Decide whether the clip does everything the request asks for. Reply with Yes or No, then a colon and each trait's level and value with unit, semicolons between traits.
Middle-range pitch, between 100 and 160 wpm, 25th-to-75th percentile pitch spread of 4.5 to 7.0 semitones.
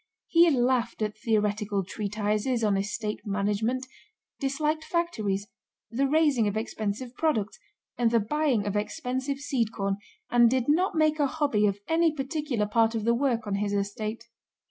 No: high, 230 Hz; average, 155 wpm; average, 4.9 semitones